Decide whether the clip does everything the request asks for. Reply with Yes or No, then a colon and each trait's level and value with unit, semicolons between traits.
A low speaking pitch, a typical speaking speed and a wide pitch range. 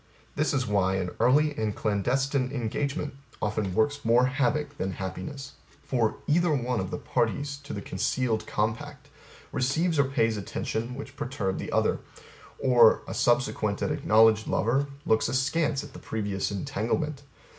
No: low, 125 Hz; average, 150 wpm; average, 4.6 semitones